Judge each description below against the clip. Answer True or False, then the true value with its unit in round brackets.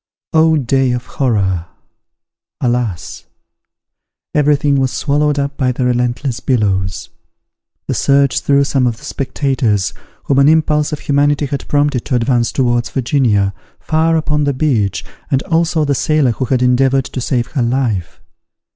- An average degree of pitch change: True (3.2 semitones)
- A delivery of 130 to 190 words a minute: True (150 wpm)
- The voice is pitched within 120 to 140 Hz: True (135 Hz)